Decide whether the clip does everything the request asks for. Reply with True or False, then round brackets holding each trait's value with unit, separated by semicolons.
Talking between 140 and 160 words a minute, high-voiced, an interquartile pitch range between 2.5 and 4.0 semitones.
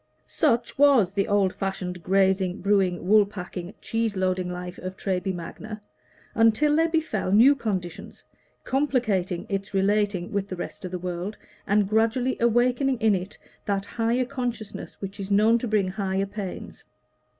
True (150 wpm; 200 Hz; 3.4 semitones)